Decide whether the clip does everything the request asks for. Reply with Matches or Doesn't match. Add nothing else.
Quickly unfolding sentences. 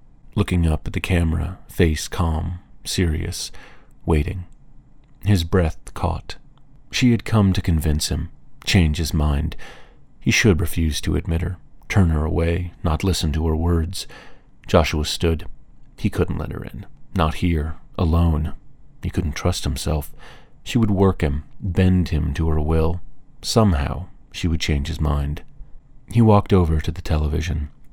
Doesn't match